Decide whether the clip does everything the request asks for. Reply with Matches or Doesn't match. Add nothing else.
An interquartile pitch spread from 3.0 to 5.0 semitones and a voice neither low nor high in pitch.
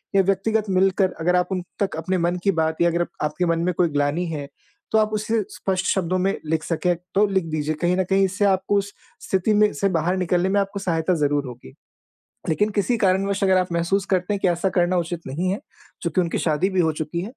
Doesn't match